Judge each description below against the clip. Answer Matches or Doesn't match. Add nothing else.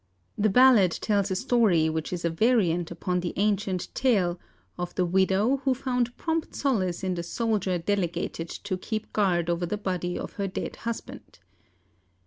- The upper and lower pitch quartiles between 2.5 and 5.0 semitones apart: Matches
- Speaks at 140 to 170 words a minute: Matches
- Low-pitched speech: Doesn't match